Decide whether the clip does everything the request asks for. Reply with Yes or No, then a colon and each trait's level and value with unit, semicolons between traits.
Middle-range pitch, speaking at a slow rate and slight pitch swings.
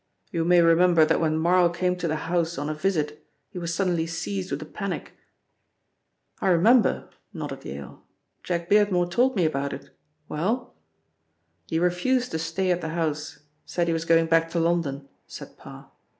No: medium, 170 Hz; average, 175 wpm; narrow, 1.9 semitones